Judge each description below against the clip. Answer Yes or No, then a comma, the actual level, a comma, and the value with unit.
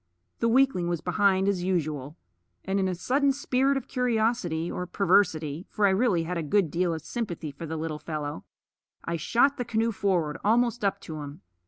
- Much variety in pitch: Yes, wide, 6.2 semitones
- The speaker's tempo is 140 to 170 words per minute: No, average, 190 wpm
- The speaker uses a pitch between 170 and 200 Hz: Yes, medium, 185 Hz